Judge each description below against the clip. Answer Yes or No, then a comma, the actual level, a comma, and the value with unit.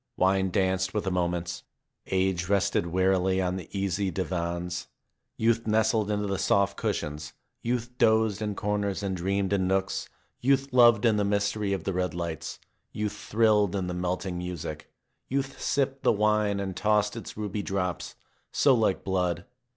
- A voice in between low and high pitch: No, low, 100 Hz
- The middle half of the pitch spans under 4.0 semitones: Yes, average, 2.7 semitones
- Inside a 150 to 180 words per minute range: Yes, average, 160 wpm